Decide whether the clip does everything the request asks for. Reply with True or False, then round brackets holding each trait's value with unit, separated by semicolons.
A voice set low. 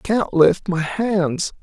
False (185 Hz)